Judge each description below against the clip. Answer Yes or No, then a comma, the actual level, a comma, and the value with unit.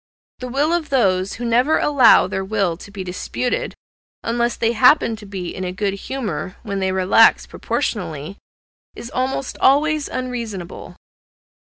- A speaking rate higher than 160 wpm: No, average, 150 wpm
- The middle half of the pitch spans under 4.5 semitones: No, average, 5.0 semitones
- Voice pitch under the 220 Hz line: No, high, 225 Hz